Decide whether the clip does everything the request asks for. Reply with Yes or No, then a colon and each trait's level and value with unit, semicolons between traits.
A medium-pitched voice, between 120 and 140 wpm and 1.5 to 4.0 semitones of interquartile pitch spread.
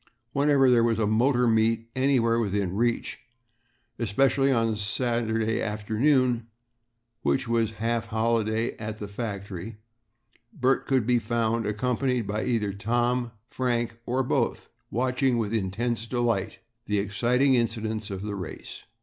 No: low, 115 Hz; slow, 135 wpm; narrow, 2.5 semitones